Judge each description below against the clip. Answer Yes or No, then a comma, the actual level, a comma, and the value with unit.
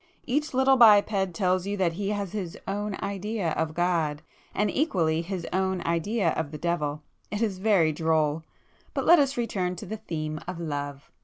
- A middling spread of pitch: Yes, average, 4.3 semitones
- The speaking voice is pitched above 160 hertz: Yes, medium, 185 Hz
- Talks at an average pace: Yes, average, 180 wpm